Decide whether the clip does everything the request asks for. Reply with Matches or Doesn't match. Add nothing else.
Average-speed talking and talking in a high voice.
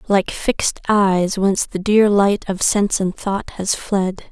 Matches